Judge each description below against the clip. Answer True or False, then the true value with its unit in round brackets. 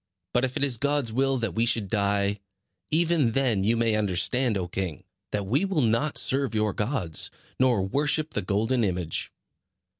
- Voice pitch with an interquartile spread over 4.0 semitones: True (5.1 semitones)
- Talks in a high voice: False (115 Hz)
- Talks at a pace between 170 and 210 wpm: True (175 wpm)